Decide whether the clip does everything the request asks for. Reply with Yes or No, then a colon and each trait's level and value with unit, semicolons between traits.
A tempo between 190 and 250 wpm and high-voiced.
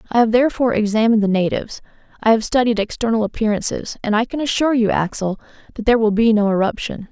Yes: average, 195 wpm; high, 220 Hz